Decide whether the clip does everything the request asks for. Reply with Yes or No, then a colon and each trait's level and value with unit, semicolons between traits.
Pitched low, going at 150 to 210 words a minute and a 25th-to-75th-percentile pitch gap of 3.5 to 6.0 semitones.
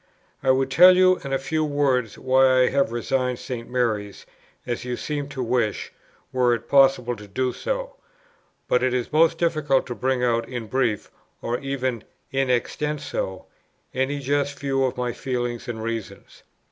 No: low, 130 Hz; average, 170 wpm; narrow, 2.5 semitones